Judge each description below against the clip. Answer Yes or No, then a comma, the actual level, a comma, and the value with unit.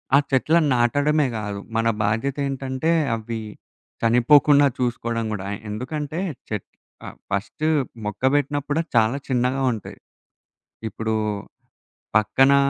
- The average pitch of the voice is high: No, low, 130 Hz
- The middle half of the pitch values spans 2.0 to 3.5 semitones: No, average, 4.2 semitones